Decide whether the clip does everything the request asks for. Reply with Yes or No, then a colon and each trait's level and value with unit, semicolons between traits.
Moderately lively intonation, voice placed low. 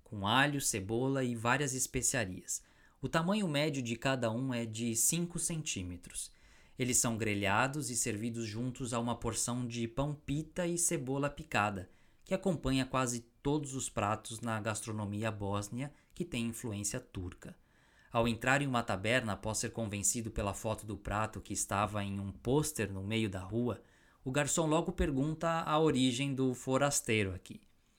Yes: average, 4.0 semitones; low, 120 Hz